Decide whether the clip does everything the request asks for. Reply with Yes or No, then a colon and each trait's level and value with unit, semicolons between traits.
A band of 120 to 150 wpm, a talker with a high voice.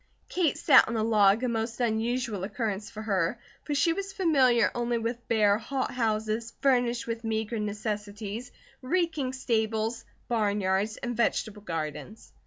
Yes: average, 145 wpm; high, 225 Hz